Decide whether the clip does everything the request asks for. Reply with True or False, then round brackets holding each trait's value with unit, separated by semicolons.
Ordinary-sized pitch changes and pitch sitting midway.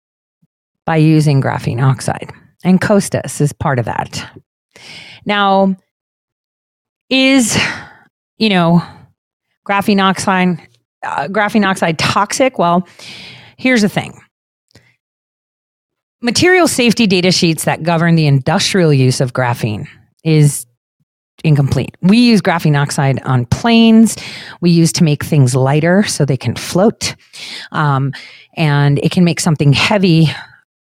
False (5.9 semitones; 165 Hz)